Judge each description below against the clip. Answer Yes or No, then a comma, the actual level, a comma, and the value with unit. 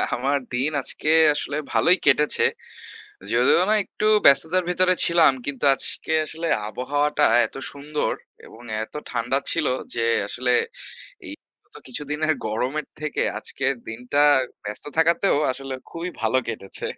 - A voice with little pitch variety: No, average, 4.0 semitones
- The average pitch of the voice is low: No, medium, 145 Hz